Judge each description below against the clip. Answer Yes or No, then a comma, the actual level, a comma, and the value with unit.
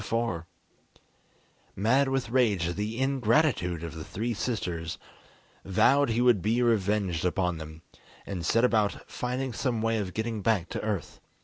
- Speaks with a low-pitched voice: Yes, low, 110 Hz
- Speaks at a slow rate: No, average, 155 wpm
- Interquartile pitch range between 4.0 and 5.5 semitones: Yes, average, 5.1 semitones